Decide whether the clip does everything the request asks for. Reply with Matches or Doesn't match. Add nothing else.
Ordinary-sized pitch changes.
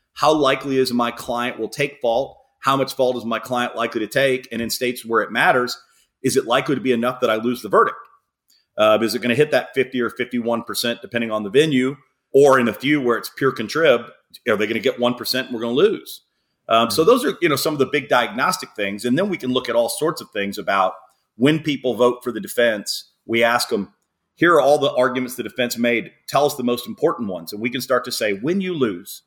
Doesn't match